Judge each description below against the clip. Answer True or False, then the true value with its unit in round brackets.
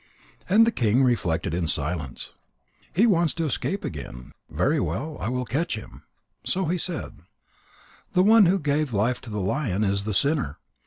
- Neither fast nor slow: True (175 wpm)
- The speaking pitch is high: False (130 Hz)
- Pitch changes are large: True (9.0 semitones)